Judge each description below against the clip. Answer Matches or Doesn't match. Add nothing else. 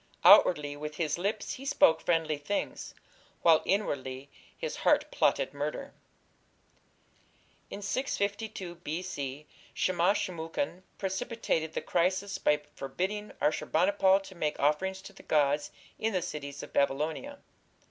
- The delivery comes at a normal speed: Doesn't match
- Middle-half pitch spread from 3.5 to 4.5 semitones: Doesn't match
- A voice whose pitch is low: Doesn't match